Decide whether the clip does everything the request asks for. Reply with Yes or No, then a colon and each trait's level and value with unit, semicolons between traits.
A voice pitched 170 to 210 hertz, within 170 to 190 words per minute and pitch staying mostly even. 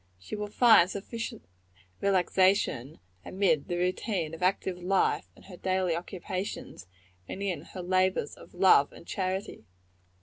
No: medium, 185 Hz; slow, 135 wpm; narrow, 1.9 semitones